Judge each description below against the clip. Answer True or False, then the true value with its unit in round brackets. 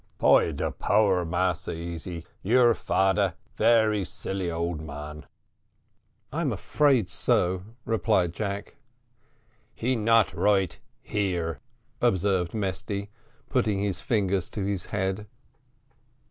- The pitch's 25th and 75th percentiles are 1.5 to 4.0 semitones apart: True (3.3 semitones)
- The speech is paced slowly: True (105 wpm)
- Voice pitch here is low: True (95 Hz)